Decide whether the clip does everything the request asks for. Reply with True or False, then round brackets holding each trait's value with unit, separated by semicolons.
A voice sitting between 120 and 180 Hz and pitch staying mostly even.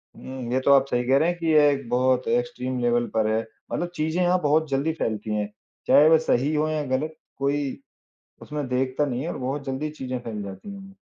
False (135 Hz; 3.8 semitones)